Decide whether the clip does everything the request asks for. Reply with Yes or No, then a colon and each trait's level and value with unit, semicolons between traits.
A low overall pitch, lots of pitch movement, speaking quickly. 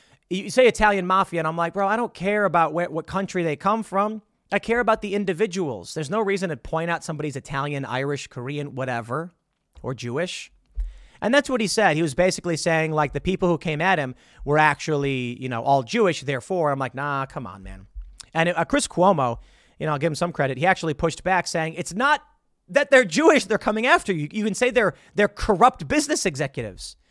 No: medium, 170 Hz; wide, 6.0 semitones; fast, 215 wpm